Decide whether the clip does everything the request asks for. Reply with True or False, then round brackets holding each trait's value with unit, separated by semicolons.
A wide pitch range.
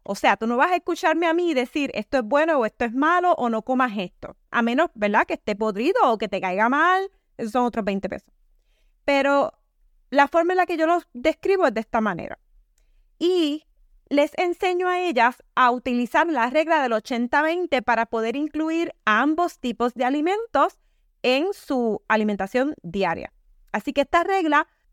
True (5.9 semitones)